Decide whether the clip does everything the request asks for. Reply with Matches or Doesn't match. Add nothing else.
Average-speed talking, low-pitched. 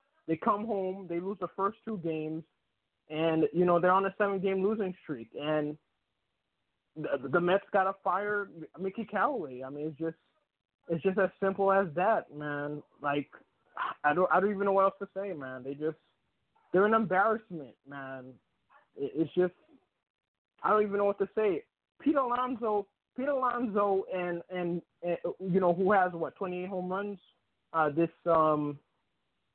Doesn't match